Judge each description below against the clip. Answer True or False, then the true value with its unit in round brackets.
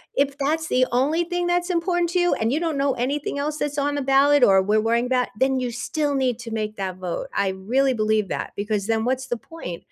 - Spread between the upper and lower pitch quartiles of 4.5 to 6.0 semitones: True (4.8 semitones)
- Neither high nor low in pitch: False (265 Hz)